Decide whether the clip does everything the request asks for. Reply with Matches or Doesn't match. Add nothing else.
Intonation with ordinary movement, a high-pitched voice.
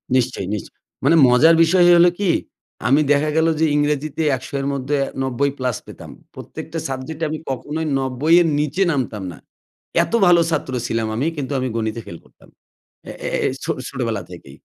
Doesn't match